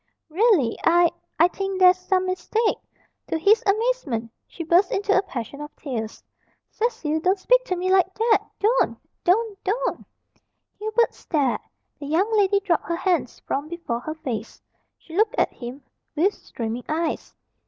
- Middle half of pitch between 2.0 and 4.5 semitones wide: No, average, 5.3 semitones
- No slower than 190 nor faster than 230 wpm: No, average, 160 wpm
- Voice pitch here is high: Yes, very high, 360 Hz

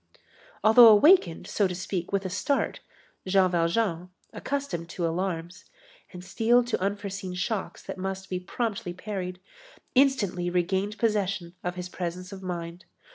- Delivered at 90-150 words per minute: Yes, average, 140 wpm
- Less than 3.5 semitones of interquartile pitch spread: Yes, average, 2.7 semitones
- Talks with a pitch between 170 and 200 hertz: Yes, medium, 185 Hz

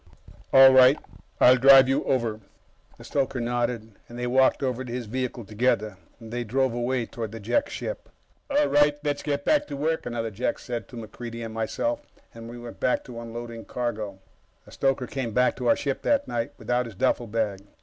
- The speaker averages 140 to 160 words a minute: No, average, 190 wpm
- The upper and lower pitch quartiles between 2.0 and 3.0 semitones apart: Yes, narrow, 2.5 semitones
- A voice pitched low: Yes, low, 120 Hz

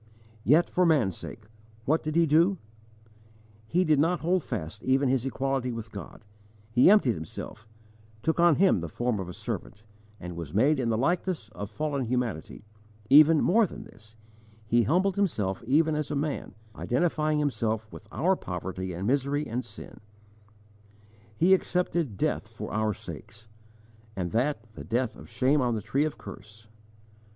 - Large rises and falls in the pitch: Yes, wide, 6.2 semitones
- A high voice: No, low, 130 Hz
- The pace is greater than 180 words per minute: No, average, 160 wpm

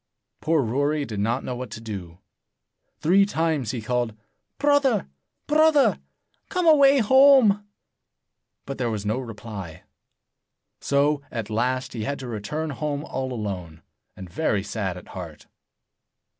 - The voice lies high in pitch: No, low, 130 Hz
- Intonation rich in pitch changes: Yes, wide, 7.4 semitones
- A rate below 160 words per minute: Yes, slow, 135 wpm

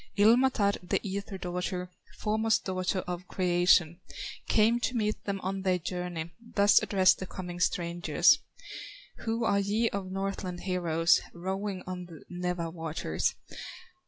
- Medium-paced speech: No, slow, 130 wpm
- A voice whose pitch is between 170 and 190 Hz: Yes, medium, 185 Hz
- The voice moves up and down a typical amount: No, narrow, 2.2 semitones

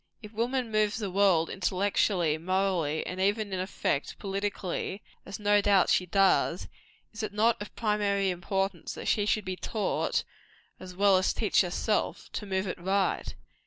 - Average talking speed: Yes, average, 160 wpm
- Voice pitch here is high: Yes, high, 195 Hz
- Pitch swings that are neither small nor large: No, narrow, 2.0 semitones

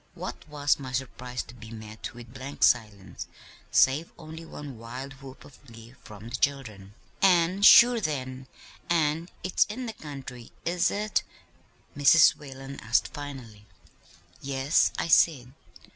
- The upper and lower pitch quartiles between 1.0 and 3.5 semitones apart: No, average, 4.6 semitones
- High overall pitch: No, low, 135 Hz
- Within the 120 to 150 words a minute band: Yes, average, 140 wpm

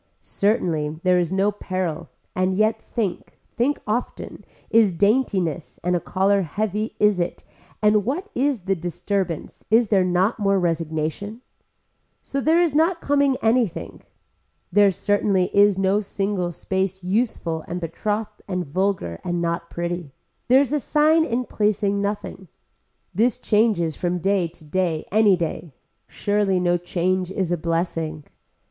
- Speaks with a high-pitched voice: Yes, high, 195 Hz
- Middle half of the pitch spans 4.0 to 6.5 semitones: No, average, 3.6 semitones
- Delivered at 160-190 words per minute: No, average, 145 wpm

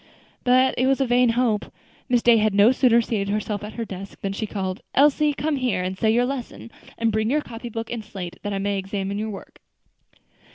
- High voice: Yes, high, 225 Hz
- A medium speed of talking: No, fast, 215 wpm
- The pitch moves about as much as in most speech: Yes, average, 3.5 semitones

